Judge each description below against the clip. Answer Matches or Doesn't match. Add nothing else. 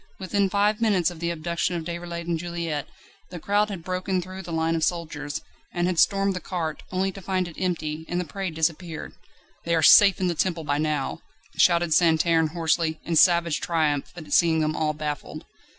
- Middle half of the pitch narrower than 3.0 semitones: Matches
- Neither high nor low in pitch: Matches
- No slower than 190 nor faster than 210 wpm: Matches